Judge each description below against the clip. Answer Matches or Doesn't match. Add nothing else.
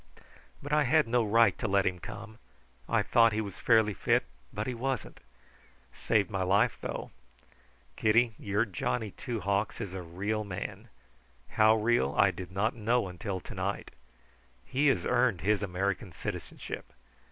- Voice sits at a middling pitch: Doesn't match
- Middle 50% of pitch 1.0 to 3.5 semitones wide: Matches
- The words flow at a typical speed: Matches